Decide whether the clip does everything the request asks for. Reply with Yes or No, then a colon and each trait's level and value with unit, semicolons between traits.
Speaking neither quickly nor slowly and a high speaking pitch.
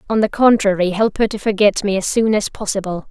No: fast, 230 wpm; high, 205 Hz